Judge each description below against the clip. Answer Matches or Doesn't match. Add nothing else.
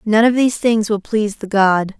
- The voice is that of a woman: Matches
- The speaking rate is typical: Doesn't match